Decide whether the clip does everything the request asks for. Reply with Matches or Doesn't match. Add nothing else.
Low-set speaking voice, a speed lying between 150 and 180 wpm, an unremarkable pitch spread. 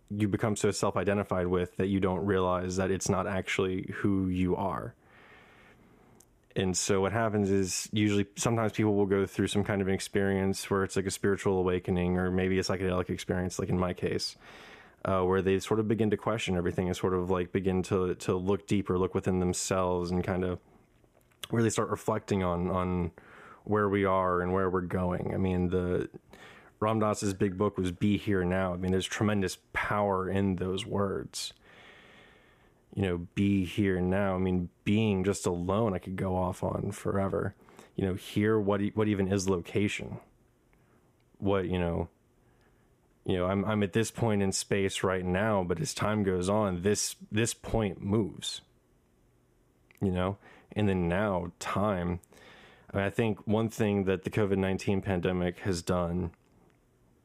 Doesn't match